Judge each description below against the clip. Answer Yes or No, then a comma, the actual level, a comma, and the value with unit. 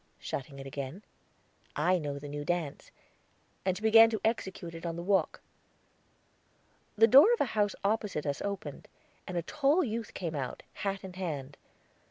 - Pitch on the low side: No, medium, 185 Hz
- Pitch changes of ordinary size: No, wide, 6.6 semitones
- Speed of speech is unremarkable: Yes, average, 170 wpm